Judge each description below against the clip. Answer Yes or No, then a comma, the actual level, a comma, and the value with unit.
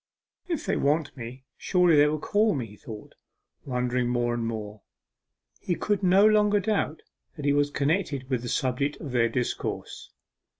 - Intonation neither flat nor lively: No, wide, 6.6 semitones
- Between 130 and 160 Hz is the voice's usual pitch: Yes, medium, 140 Hz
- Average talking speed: Yes, average, 170 wpm